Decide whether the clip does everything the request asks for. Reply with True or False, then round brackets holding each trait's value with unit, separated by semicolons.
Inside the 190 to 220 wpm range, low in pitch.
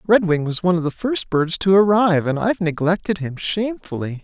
False (200 wpm; 175 Hz)